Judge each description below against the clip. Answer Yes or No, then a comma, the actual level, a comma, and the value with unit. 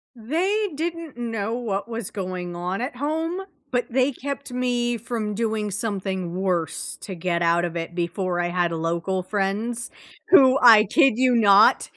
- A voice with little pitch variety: No, wide, 5.4 semitones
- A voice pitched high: Yes, high, 215 Hz